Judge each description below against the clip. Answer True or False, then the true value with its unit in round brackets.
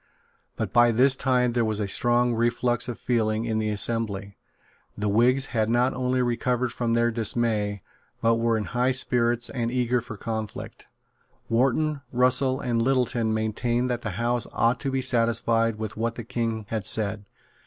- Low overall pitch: True (120 Hz)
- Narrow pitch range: True (1.9 semitones)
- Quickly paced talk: False (170 wpm)